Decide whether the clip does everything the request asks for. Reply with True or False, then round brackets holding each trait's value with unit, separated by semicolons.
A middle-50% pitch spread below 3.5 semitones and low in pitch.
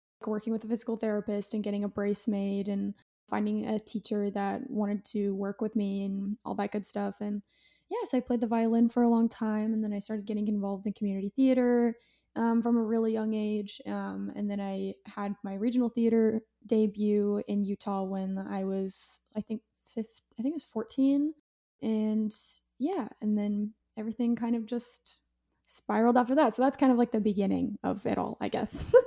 False (2.4 semitones; 215 Hz)